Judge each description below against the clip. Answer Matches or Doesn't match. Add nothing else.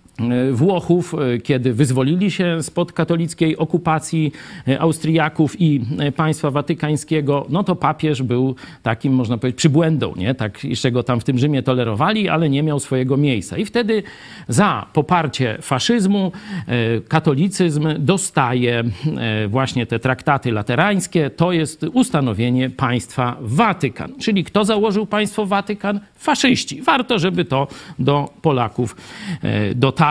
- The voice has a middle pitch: Matches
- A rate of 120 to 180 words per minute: Matches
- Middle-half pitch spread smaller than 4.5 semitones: Doesn't match